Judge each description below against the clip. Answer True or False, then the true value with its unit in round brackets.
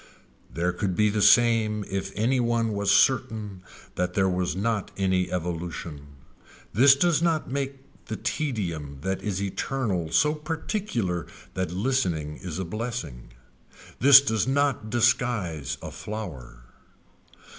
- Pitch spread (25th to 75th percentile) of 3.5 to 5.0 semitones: False (5.6 semitones)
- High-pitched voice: False (105 Hz)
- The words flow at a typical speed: False (130 wpm)